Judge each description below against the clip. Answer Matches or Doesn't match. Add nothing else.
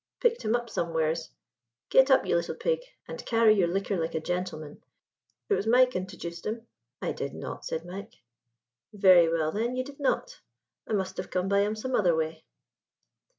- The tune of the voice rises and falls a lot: Matches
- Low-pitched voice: Doesn't match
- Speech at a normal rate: Matches